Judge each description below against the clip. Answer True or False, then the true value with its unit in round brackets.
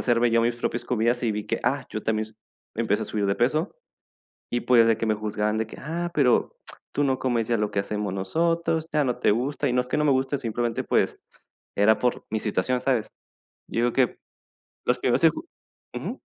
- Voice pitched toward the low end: True (120 Hz)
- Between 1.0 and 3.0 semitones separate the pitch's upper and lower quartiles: False (3.4 semitones)